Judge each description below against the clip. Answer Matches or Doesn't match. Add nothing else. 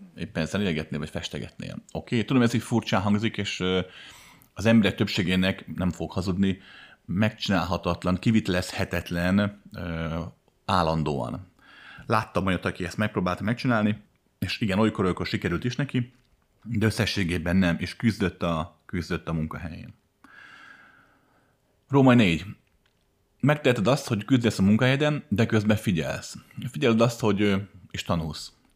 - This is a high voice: Doesn't match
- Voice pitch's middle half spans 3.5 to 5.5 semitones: Matches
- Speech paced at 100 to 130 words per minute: Matches